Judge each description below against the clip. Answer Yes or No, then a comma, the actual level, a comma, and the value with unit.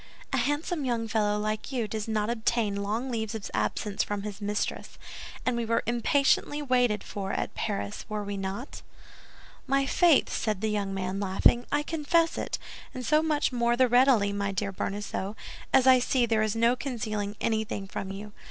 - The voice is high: Yes, high, 220 Hz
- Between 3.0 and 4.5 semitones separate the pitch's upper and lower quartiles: Yes, average, 3.7 semitones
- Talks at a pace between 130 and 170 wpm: No, average, 180 wpm